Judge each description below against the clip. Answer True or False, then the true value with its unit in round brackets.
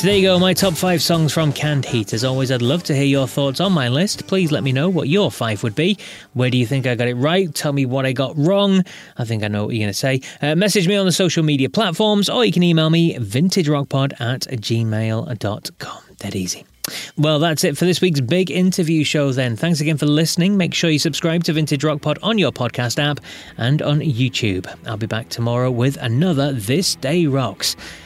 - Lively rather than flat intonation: True (5.8 semitones)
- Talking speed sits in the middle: False (235 wpm)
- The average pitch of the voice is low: False (150 Hz)